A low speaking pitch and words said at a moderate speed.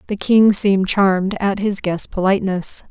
No: high, 195 Hz; average, 165 wpm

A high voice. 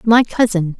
Yes: high, 205 Hz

